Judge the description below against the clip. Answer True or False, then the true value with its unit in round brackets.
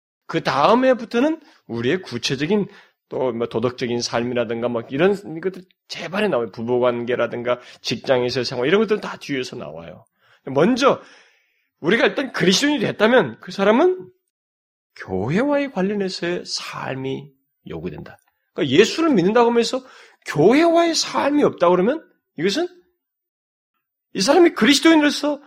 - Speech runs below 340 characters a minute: True (320 characters per minute)